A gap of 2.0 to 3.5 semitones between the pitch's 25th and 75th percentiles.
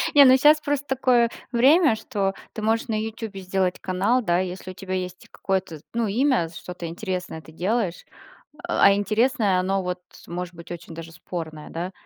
No: average, 4.6 semitones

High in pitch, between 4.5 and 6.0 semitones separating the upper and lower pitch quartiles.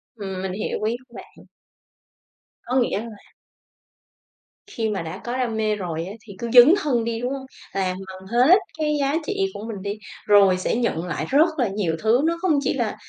Yes: high, 225 Hz; average, 5.1 semitones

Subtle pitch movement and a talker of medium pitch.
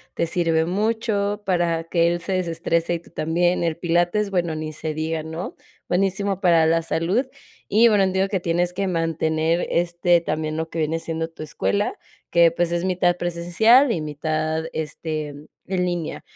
Yes: narrow, 2.1 semitones; medium, 170 Hz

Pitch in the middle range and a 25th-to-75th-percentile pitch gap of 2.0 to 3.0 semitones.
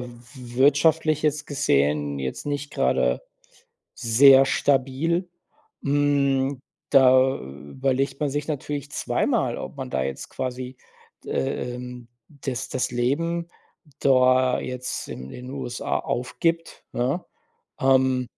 No: low, 130 Hz; narrow, 2.5 semitones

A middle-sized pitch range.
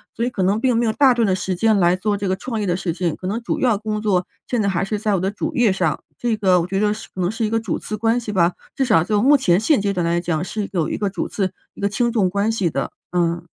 Yes: average, 3.6 semitones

